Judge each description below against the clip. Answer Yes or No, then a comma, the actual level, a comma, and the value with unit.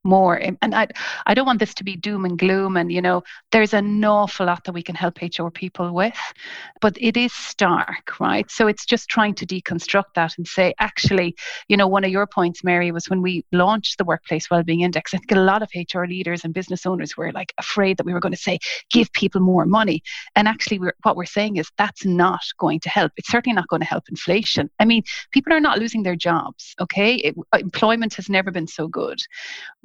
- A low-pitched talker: No, high, 190 Hz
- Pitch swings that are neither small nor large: Yes, average, 3.3 semitones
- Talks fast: Yes, fast, 230 wpm